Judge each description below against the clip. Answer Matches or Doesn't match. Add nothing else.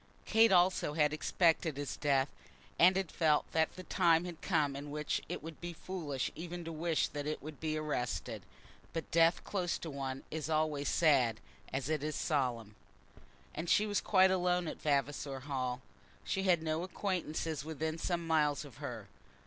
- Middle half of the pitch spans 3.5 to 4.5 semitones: Doesn't match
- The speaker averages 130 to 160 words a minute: Doesn't match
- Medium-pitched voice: Matches